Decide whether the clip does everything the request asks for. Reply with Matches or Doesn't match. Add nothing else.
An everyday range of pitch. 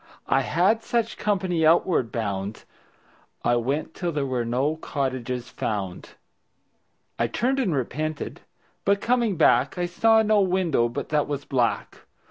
Doesn't match